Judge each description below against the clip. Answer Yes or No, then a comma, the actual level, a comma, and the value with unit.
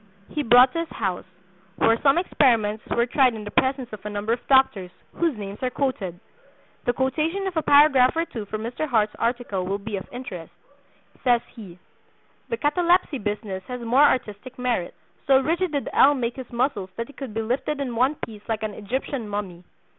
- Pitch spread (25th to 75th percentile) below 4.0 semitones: No, average, 4.7 semitones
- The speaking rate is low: No, average, 195 wpm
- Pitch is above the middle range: Yes, high, 245 Hz